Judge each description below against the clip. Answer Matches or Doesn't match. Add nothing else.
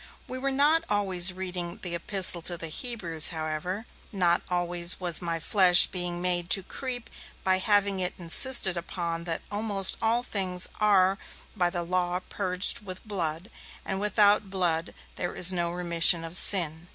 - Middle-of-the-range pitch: Matches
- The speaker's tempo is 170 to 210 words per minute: Doesn't match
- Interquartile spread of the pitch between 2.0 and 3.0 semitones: Matches